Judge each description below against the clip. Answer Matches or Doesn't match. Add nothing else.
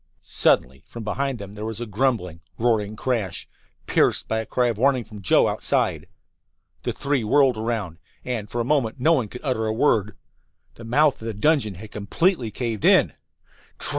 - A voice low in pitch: Matches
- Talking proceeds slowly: Doesn't match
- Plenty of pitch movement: Doesn't match